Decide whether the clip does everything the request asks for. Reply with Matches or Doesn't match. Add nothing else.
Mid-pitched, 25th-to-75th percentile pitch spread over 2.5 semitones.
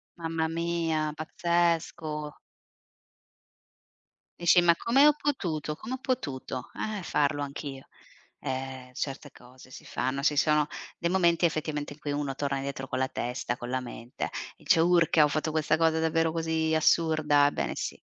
Matches